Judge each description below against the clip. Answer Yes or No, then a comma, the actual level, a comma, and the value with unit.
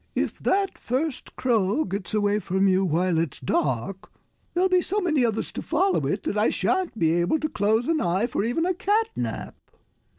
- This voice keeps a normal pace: Yes, average, 195 wpm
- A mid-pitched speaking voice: No, high, 225 Hz